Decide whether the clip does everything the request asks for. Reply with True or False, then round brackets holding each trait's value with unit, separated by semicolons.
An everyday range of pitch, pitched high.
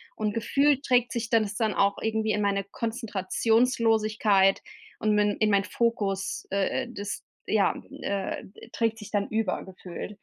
False (2.3 semitones; 215 Hz)